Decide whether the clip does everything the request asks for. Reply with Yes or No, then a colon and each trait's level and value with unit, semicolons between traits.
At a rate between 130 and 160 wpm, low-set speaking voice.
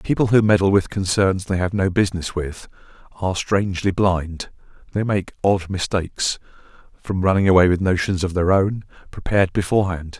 Yes: average, 155 wpm; very low, 95 Hz